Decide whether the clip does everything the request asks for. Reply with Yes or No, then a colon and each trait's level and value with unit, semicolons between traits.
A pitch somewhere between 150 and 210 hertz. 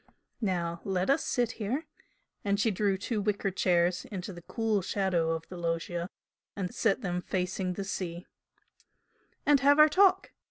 Yes: high, 190 Hz